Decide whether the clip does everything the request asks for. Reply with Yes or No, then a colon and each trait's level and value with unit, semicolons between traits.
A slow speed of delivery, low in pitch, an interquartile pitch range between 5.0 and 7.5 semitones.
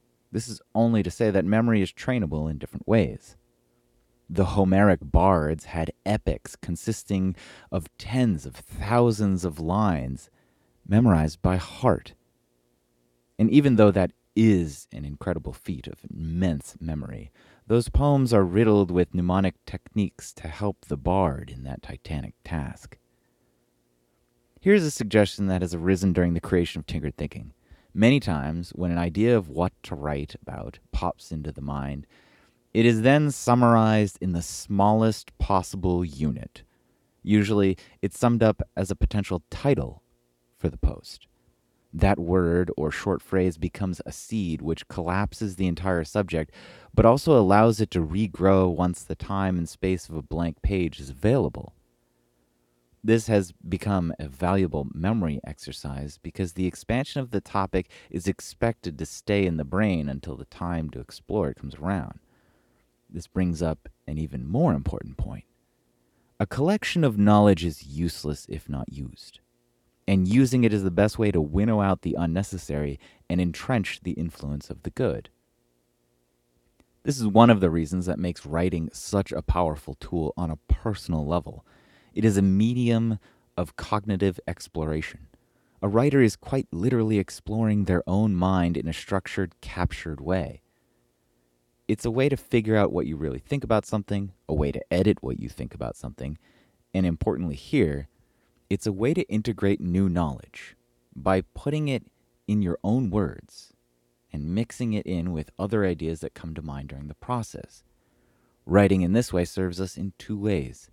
No: average, 160 wpm; very low, 90 Hz; average, 5.3 semitones